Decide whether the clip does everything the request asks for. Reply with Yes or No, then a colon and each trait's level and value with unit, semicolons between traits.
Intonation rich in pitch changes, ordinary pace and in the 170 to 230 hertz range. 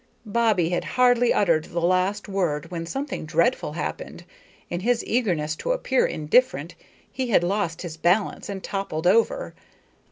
Yes: wide, 5.8 semitones; average, 150 wpm; high, 190 Hz